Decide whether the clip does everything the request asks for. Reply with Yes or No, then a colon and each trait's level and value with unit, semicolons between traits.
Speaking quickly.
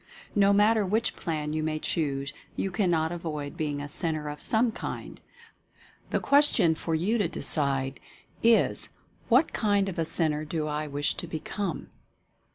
No: average, 165 wpm